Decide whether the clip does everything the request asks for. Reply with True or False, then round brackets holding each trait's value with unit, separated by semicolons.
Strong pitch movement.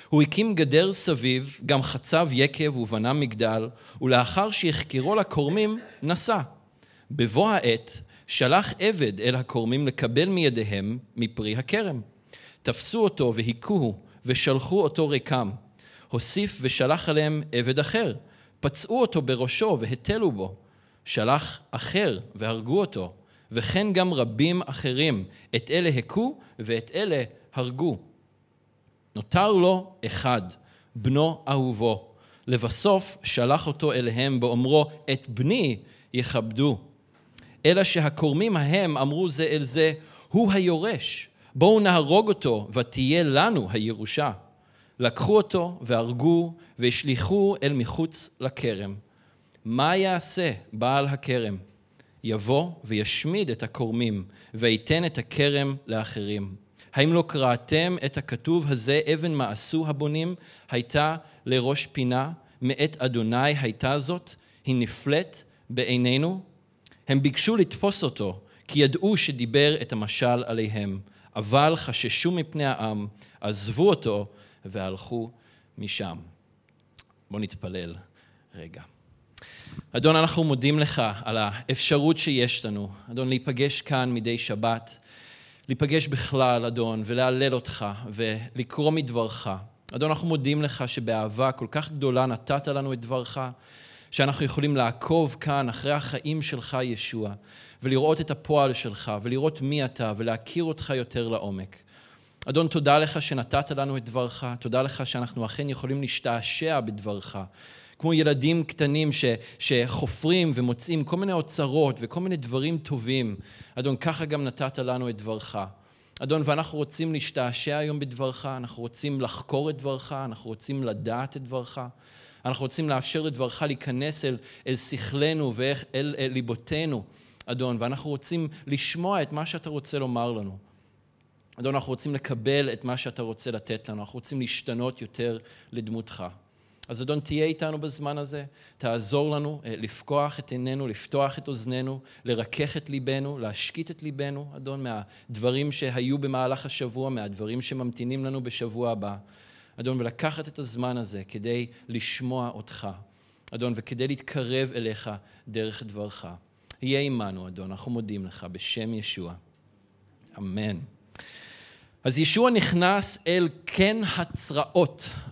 False (4.4 semitones)